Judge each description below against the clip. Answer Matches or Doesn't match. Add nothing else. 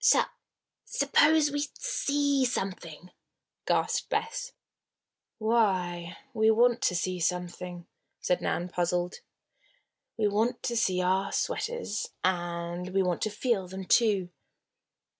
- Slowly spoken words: Matches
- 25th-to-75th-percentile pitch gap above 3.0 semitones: Matches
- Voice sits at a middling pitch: Doesn't match